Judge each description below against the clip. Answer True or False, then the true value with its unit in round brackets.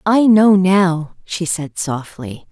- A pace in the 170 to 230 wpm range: False (145 wpm)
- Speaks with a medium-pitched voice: True (175 Hz)